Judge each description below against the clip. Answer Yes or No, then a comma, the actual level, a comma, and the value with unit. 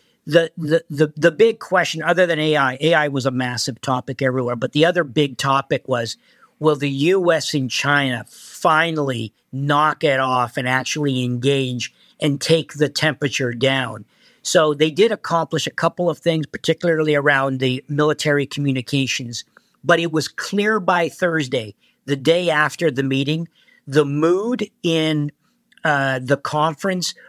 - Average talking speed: Yes, average, 150 wpm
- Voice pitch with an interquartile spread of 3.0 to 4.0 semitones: Yes, average, 3.4 semitones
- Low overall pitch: No, medium, 150 Hz